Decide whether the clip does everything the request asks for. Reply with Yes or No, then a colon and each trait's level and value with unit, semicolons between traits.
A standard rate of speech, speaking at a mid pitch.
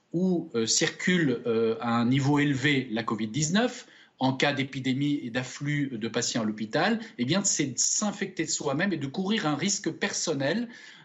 Yes: average, 170 wpm; medium, 145 Hz